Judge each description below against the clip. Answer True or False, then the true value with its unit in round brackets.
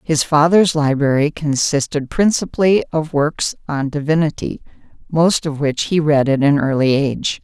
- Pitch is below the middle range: False (150 Hz)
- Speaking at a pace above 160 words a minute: False (145 wpm)